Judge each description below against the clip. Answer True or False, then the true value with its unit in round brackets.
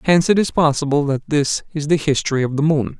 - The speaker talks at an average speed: False (240 wpm)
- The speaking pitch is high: False (150 Hz)